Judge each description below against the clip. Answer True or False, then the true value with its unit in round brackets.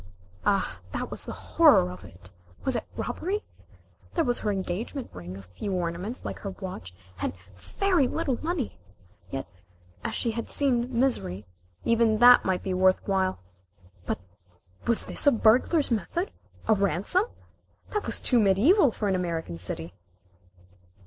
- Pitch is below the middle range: False (210 Hz)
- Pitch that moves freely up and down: True (6.2 semitones)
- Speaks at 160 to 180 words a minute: False (150 wpm)